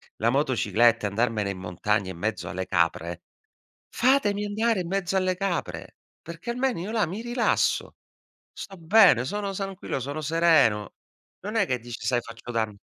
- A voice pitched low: No, medium, 145 Hz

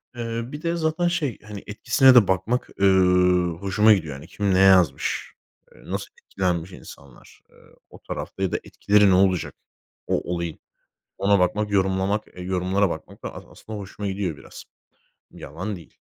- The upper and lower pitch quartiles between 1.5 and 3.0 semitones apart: Yes, average, 2.7 semitones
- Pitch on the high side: No, very low, 95 Hz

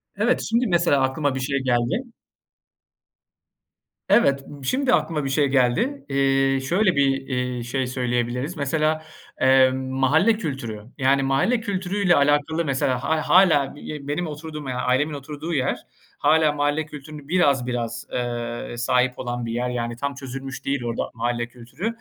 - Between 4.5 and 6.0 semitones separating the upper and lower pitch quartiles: No, average, 3.8 semitones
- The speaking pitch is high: No, medium, 140 Hz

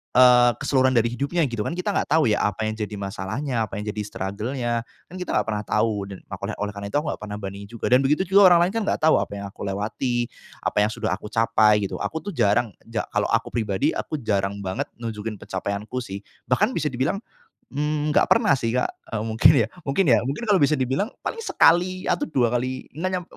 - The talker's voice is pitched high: No, low, 120 Hz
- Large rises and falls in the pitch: Yes, wide, 6.1 semitones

